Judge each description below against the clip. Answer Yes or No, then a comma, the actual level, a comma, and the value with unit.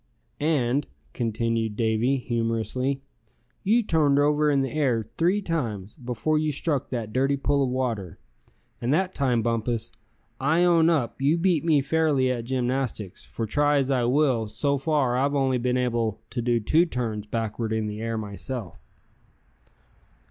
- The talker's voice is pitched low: Yes, low, 130 Hz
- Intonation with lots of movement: No, average, 4.1 semitones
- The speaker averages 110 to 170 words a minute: Yes, average, 155 wpm